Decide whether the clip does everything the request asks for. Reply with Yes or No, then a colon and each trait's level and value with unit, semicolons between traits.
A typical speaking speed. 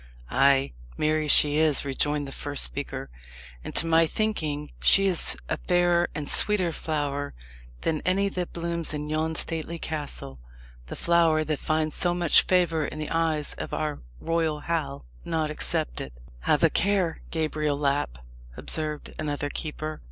Yes: average, 150 wpm